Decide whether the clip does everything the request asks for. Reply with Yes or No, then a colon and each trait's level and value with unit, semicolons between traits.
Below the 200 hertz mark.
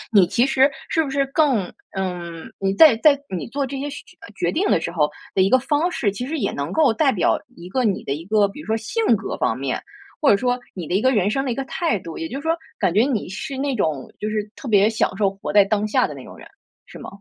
No: high, 220 Hz